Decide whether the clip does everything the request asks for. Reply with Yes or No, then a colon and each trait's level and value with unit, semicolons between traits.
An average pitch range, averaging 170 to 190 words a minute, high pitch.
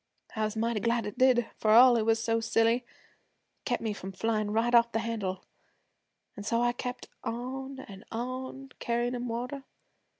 No: narrow, 1.8 semitones; average, 180 wpm; high, 235 Hz